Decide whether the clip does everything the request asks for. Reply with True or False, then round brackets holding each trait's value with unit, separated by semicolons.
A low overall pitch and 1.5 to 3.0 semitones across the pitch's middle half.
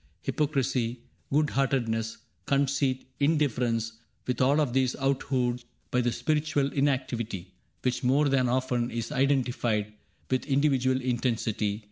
True (130 Hz; 2.5 semitones)